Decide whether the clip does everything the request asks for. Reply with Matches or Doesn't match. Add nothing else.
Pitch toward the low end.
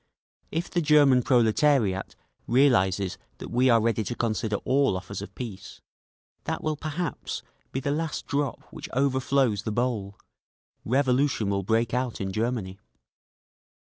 Matches